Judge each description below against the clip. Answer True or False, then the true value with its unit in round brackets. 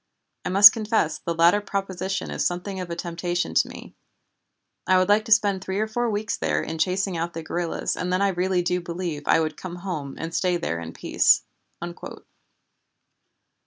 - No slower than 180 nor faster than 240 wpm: True (190 wpm)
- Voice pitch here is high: False (180 Hz)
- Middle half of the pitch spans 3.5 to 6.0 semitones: False (2.7 semitones)